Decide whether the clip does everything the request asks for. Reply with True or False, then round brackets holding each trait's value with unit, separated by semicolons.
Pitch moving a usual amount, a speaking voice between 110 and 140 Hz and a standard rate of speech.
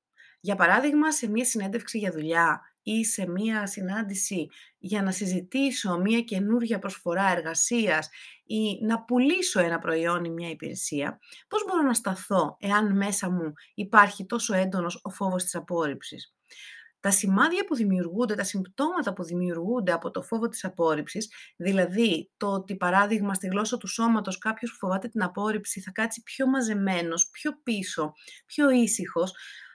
False (4.0 semitones; 200 Hz; 150 wpm)